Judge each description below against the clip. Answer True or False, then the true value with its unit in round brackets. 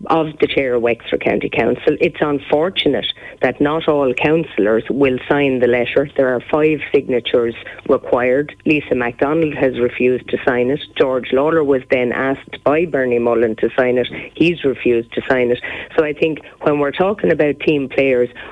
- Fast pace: False (175 wpm)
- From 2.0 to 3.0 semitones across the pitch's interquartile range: False (3.6 semitones)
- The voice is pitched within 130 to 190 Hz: True (135 Hz)